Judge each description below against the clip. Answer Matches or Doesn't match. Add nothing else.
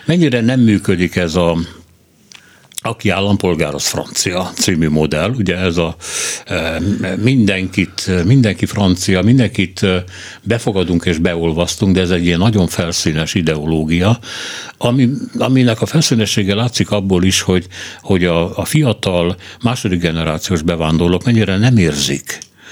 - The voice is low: Matches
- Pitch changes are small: Doesn't match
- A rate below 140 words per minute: Matches